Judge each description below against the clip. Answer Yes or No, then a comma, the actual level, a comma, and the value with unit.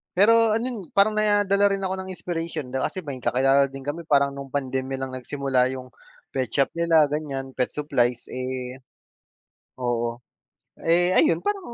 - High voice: No, medium, 140 Hz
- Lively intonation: Yes, wide, 6.1 semitones